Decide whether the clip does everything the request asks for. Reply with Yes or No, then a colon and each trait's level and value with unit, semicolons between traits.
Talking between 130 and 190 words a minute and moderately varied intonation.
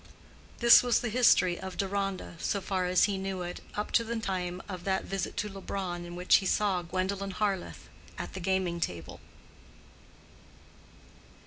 No: average, 160 wpm; narrow, 1.9 semitones